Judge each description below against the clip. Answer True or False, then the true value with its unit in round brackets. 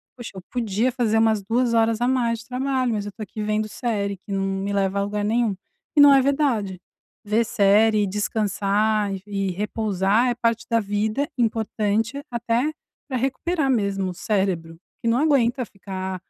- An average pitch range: True (3.1 semitones)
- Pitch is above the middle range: True (220 Hz)